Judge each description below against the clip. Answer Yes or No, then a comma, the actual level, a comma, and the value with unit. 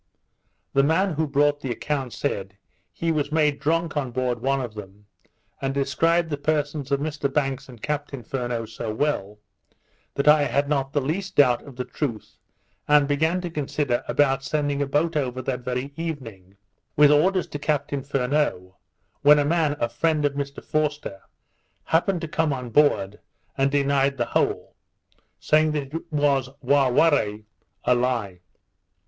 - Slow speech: No, average, 165 wpm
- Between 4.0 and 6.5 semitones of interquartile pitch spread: No, average, 3.0 semitones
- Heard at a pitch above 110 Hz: Yes, medium, 140 Hz